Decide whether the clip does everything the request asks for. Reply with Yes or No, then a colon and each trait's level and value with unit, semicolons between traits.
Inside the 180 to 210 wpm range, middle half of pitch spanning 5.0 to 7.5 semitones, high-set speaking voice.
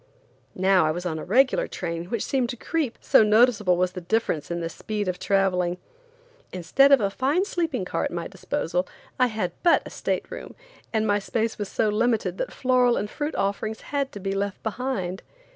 Yes: average, 200 wpm; wide, 5.4 semitones; high, 210 Hz